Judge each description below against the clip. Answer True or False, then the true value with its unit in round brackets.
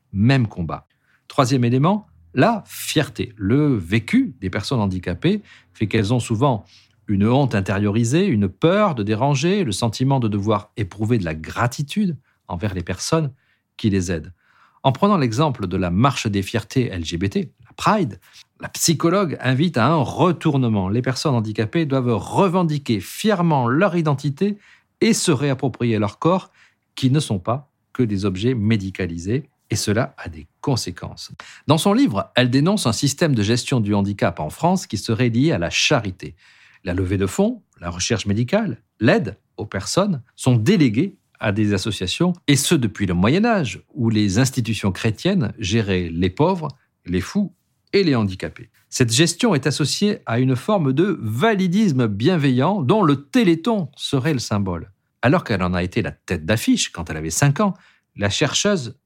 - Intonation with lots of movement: True (7.4 semitones)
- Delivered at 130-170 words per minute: True (165 wpm)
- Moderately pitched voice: False (120 Hz)